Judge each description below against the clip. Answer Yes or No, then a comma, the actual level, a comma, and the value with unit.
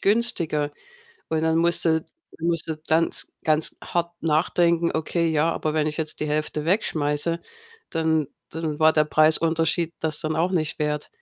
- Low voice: No, medium, 160 Hz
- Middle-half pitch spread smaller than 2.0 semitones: Yes, narrow, 1.4 semitones